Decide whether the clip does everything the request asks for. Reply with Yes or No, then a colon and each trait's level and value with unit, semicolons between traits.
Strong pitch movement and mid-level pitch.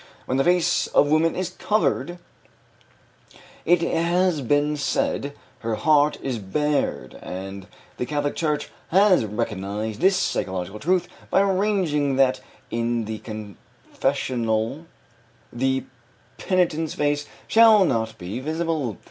Yes: wide, 6.9 semitones; medium, 145 Hz